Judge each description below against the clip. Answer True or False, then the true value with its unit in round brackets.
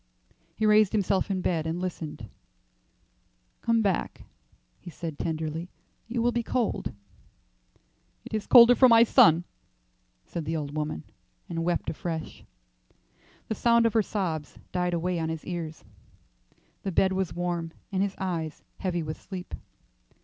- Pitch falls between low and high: True (180 Hz)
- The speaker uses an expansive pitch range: False (4.4 semitones)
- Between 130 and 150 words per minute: True (145 wpm)